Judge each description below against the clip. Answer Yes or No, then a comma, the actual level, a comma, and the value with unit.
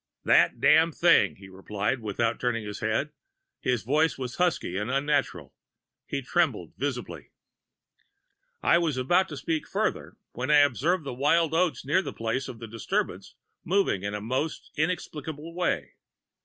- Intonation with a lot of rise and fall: Yes, wide, 5.9 semitones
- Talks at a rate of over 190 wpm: No, average, 155 wpm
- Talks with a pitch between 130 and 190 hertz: Yes, medium, 140 Hz